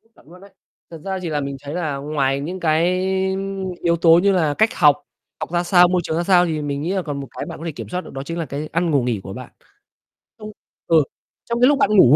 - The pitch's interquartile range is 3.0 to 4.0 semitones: Yes, average, 3.7 semitones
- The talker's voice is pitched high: No, medium, 165 Hz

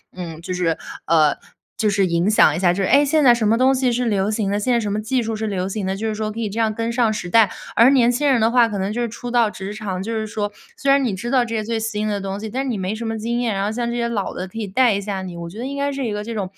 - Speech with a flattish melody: No, average, 3.3 semitones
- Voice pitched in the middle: No, high, 220 Hz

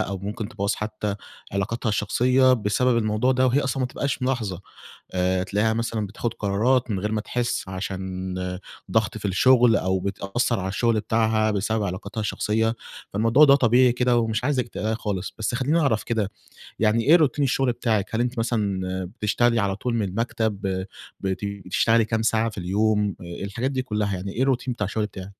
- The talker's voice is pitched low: Yes, low, 110 Hz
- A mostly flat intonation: No, average, 3.4 semitones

